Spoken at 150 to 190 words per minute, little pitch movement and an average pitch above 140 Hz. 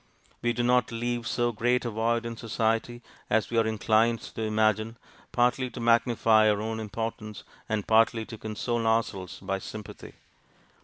No: average, 160 wpm; narrow, 1.5 semitones; low, 115 Hz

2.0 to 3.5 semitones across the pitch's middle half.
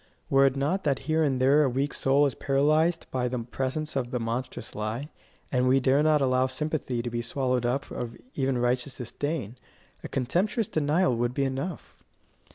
Yes: average, 2.9 semitones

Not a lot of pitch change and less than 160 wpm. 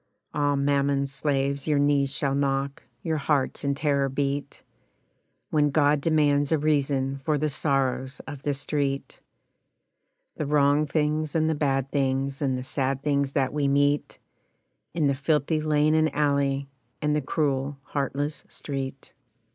Yes: narrow, 1.4 semitones; average, 145 wpm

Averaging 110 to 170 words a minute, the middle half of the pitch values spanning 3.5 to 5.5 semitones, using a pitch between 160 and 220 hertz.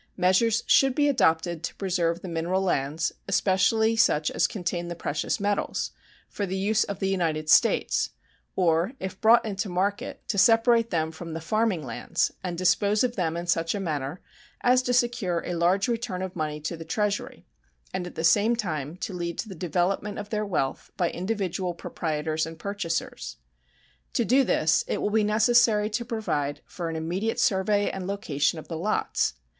No: average, 180 wpm; average, 4.2 semitones; medium, 185 Hz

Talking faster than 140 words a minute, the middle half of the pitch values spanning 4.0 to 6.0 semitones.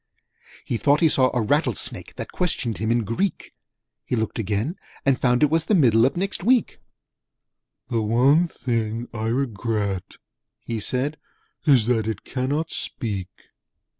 Yes: average, 150 wpm; average, 4.7 semitones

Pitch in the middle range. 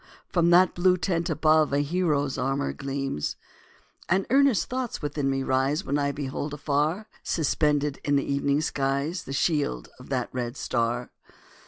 Yes: medium, 145 Hz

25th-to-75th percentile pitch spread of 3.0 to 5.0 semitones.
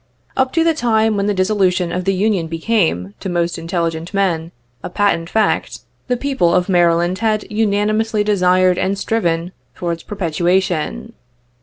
Yes: average, 3.8 semitones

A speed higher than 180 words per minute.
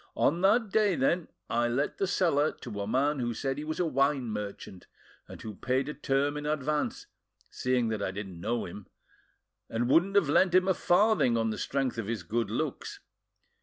Yes: average, 200 wpm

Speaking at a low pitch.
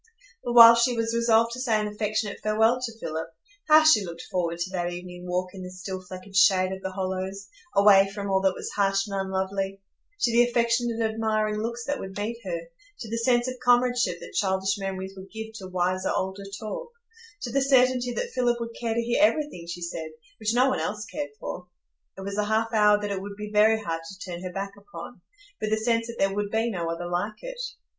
No: high, 210 Hz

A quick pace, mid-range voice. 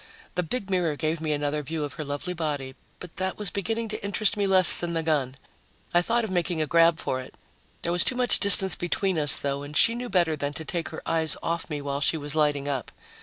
Yes: fast, 245 wpm; medium, 165 Hz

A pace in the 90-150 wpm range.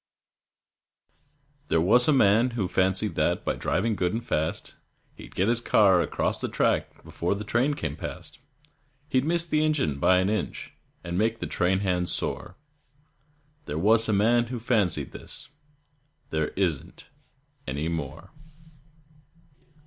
Yes: average, 145 wpm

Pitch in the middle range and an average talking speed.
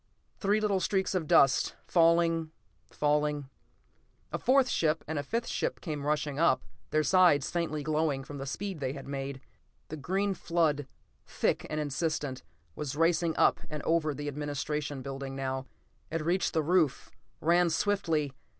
Yes: medium, 155 Hz; average, 150 wpm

